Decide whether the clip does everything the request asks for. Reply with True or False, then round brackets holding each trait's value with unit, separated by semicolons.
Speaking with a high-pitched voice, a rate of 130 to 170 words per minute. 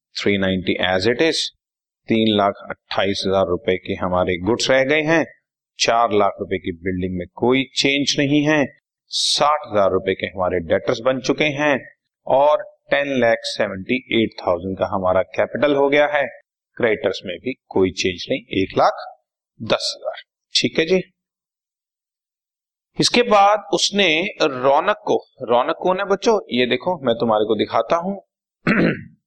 False (125 Hz; 155 wpm)